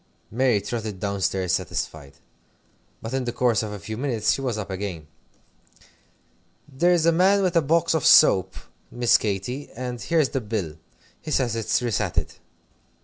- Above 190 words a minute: No, average, 165 wpm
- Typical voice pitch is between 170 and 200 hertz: No, low, 115 Hz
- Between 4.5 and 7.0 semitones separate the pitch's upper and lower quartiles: Yes, average, 5.3 semitones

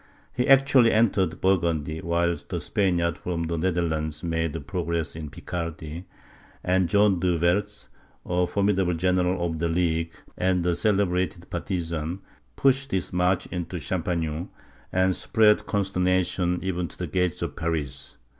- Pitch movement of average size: No, narrow, 2.2 semitones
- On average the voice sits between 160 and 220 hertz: No, very low, 90 Hz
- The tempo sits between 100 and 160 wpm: Yes, slow, 135 wpm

